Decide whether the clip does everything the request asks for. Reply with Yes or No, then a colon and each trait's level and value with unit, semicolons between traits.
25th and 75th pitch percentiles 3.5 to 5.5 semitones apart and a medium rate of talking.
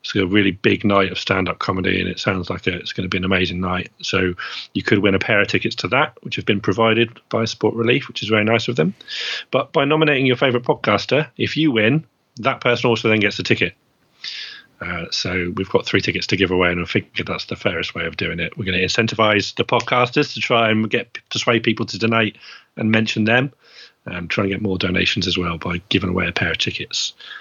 No: average, 3.9 semitones; fast, 240 wpm